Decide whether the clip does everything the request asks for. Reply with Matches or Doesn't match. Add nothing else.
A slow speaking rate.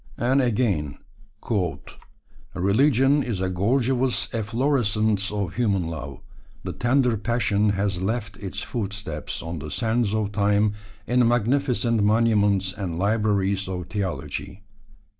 Matches